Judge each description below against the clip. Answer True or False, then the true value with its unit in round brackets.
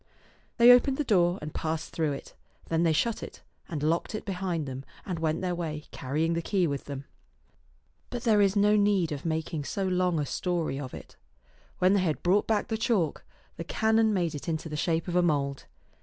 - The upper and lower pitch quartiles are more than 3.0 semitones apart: True (4.4 semitones)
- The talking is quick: True (210 wpm)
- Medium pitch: True (170 Hz)